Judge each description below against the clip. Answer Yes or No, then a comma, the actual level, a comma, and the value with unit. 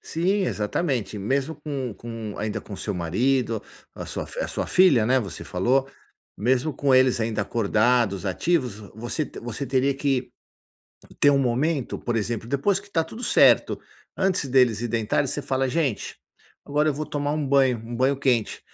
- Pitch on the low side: Yes, low, 130 Hz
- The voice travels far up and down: No, average, 3.9 semitones